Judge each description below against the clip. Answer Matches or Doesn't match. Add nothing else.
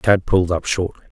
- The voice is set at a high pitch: Doesn't match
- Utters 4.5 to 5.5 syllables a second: Doesn't match